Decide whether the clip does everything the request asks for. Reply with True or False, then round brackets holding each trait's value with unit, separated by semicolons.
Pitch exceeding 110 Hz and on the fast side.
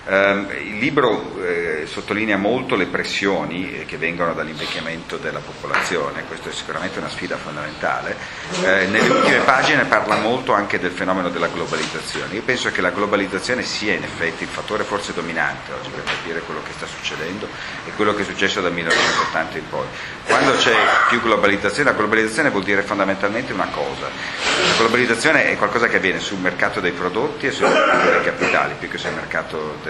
False (95 Hz; 185 wpm)